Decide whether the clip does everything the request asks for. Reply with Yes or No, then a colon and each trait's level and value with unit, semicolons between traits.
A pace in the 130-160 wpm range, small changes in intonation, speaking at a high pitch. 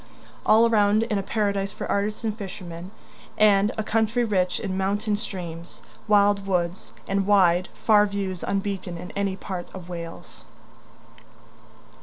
Yes: average, 140 wpm; narrow, 2.3 semitones; high, 200 Hz